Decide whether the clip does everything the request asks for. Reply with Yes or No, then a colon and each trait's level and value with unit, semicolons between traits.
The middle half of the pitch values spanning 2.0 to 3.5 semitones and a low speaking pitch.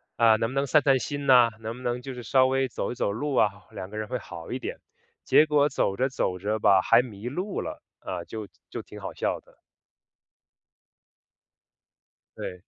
No: average, 3.9 semitones; low, 120 Hz